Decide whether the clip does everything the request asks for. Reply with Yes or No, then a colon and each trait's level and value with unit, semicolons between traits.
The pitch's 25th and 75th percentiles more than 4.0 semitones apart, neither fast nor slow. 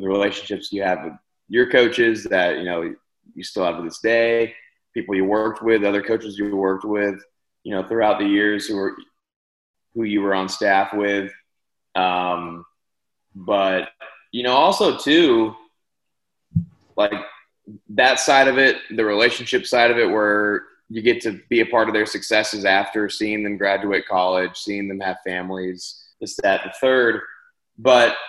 No: average, 2.7 semitones; average, 165 wpm